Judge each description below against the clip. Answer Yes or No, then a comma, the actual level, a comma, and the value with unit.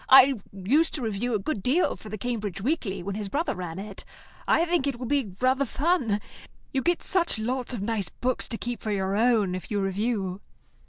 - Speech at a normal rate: No, fast, 210 wpm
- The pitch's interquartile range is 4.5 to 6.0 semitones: Yes, average, 5.1 semitones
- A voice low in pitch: No, high, 230 Hz